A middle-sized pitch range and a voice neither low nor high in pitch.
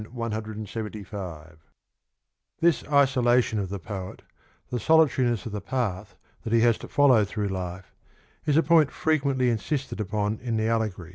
No: average, 4.3 semitones; low, 110 Hz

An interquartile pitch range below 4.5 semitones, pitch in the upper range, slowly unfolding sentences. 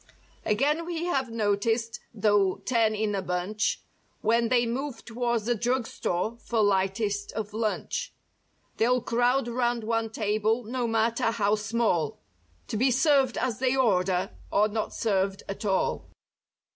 No: average, 2.8 semitones; high, 225 Hz; average, 145 wpm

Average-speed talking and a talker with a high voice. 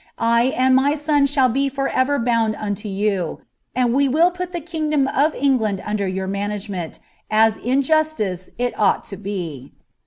Yes: average, 175 wpm; high, 240 Hz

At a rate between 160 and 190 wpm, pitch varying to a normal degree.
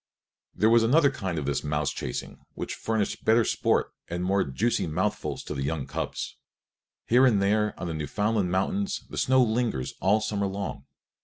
Yes: average, 175 wpm; average, 4.6 semitones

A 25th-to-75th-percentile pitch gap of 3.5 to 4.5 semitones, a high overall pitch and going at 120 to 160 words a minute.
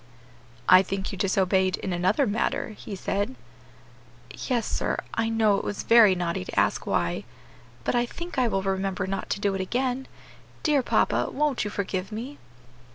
No: average, 4.0 semitones; high, 200 Hz; average, 170 wpm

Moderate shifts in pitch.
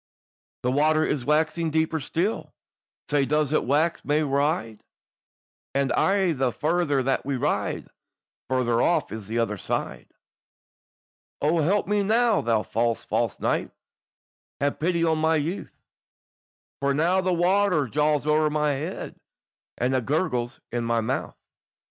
Yes: average, 4.2 semitones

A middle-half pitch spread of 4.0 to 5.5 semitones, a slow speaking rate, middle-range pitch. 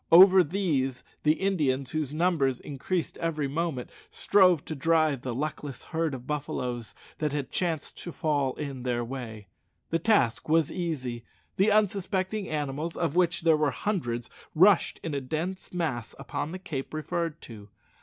No: average, 4.4 semitones; average, 155 wpm; medium, 155 Hz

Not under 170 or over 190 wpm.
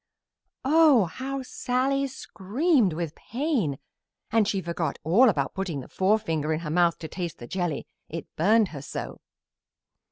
No: average, 150 wpm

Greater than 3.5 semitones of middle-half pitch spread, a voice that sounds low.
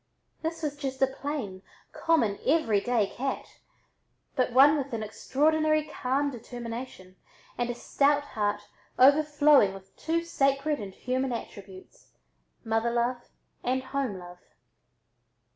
No: average, 4.6 semitones; very high, 260 Hz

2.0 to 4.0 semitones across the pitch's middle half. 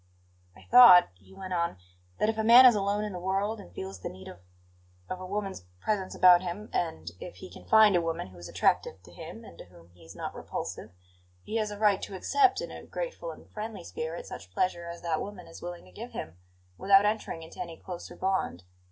No: average, 4.5 semitones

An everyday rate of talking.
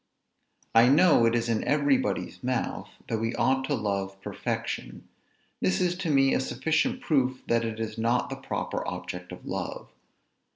Yes: average, 170 wpm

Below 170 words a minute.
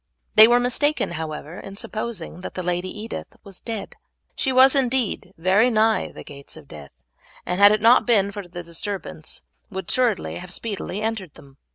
No: average, 180 wpm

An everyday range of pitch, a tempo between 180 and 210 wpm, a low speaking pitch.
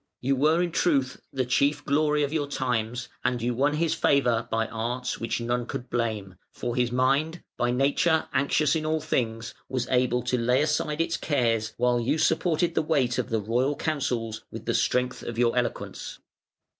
Yes: average, 3.7 semitones; average, 185 wpm; low, 125 Hz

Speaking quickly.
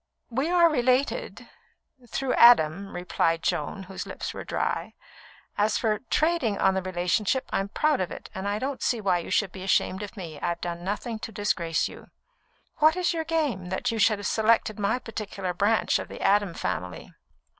No: average, 185 wpm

